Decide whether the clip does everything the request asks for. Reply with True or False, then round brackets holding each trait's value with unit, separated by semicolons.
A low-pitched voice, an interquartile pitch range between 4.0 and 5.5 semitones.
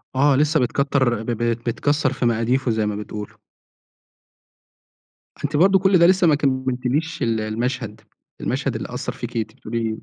True (125 Hz; 4.3 semitones)